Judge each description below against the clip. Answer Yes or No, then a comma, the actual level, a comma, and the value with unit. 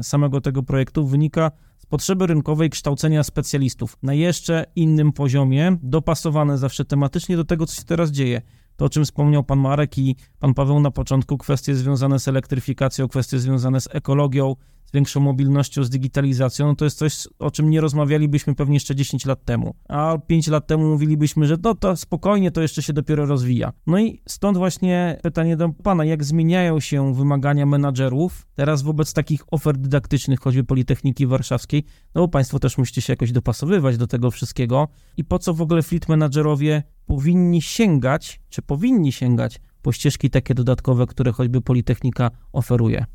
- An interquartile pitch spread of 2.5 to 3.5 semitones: Yes, average, 2.9 semitones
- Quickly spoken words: Yes, fast, 170 wpm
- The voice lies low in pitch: No, medium, 145 Hz